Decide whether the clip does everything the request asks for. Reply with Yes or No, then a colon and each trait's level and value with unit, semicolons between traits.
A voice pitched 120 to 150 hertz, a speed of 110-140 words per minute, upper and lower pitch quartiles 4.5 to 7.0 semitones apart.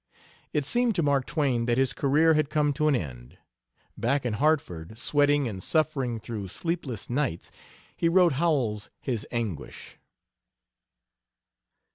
Yes: low, 135 Hz; slow, 135 wpm; average, 5.1 semitones